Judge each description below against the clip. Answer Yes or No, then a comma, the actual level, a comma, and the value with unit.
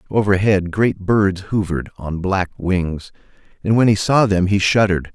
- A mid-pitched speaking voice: No, very low, 95 Hz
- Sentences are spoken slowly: No, average, 165 wpm